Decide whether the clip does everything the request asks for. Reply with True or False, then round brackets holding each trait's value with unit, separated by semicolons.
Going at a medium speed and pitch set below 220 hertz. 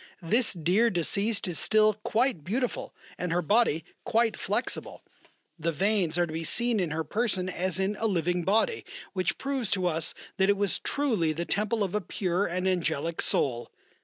True (180 wpm; 190 Hz)